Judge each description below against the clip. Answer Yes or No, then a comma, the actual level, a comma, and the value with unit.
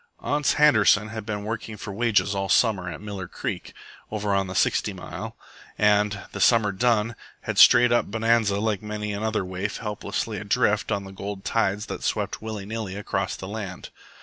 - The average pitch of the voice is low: Yes, low, 105 Hz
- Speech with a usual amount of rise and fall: No, narrow, 1.9 semitones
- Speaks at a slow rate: No, average, 175 wpm